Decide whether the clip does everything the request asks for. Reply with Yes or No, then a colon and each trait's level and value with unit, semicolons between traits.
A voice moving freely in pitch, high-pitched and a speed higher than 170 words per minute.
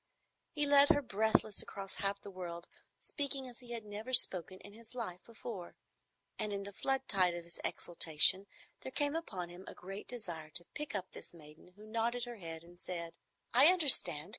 Yes: wide, 5.8 semitones; high, 205 Hz; average, 190 wpm